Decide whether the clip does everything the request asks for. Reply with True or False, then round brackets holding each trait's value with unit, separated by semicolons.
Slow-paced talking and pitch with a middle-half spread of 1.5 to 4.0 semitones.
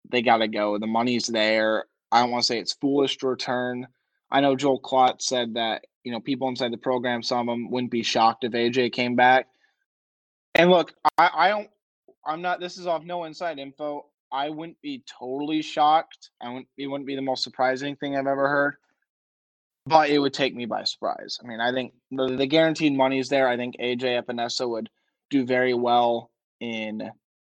False (200 wpm; 3.2 semitones)